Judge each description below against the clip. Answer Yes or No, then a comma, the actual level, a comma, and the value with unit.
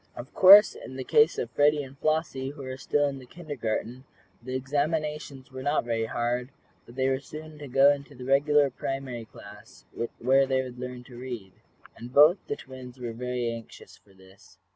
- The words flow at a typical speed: Yes, average, 190 wpm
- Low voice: Yes, low, 130 Hz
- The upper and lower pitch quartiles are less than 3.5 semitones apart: Yes, average, 2.8 semitones